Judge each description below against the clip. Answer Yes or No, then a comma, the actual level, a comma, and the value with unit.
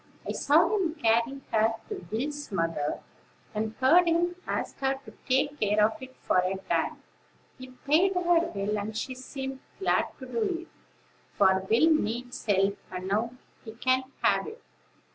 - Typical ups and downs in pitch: No, wide, 6.9 semitones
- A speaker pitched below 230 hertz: No, very high, 255 Hz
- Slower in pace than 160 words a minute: No, average, 165 wpm